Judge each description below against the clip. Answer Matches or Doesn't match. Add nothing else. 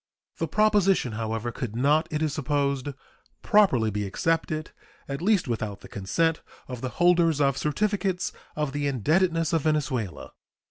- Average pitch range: Matches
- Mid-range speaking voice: Matches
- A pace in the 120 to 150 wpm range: Matches